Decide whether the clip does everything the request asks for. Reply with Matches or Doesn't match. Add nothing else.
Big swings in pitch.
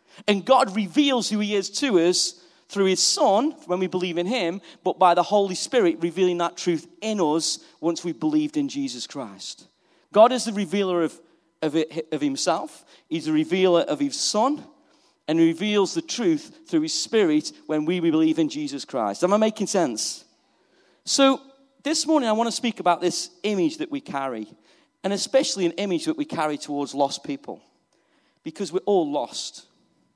Matches